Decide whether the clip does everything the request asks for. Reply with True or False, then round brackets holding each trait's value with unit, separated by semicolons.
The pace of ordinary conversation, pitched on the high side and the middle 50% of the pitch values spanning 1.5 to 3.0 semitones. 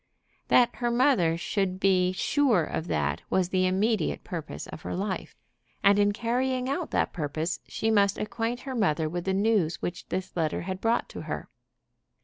False (175 wpm; 195 Hz; 4.7 semitones)